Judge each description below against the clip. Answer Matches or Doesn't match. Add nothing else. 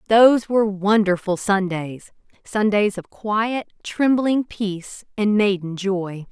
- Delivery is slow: Matches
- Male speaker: Doesn't match